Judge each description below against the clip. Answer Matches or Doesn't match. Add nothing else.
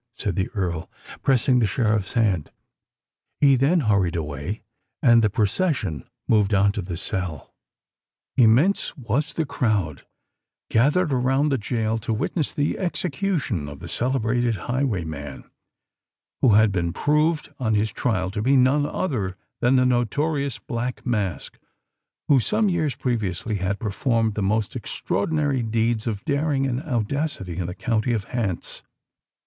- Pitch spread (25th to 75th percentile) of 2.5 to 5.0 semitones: Doesn't match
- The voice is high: Doesn't match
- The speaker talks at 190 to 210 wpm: Doesn't match